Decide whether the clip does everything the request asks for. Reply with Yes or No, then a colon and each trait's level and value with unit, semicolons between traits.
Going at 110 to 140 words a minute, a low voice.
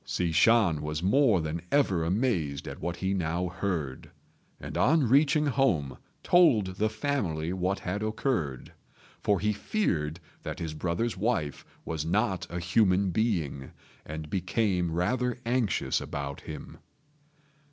Yes: slow, 135 wpm; very low, 95 Hz